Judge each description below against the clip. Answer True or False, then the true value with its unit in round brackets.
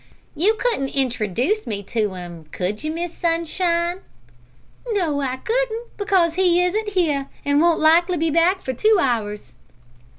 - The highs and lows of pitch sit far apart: True (6.1 semitones)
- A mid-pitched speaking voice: False (330 Hz)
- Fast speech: False (145 wpm)